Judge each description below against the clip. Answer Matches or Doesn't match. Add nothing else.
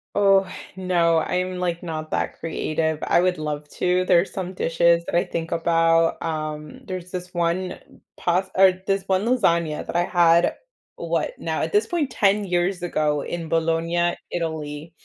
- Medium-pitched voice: Matches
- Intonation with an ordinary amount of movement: Doesn't match